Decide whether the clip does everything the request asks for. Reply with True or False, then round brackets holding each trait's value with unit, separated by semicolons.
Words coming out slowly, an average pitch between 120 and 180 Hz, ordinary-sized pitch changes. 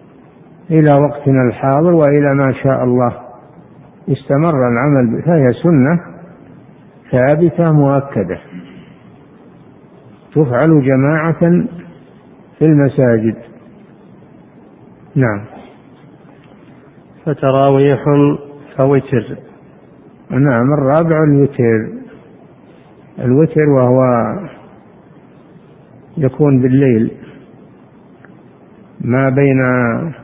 True (60 wpm; 140 Hz; 3.1 semitones)